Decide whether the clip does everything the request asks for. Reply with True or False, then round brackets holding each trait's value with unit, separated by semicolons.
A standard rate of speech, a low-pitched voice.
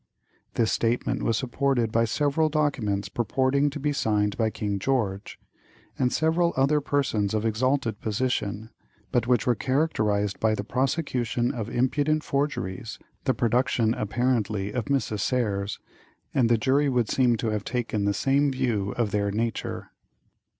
True (150 wpm; 120 Hz)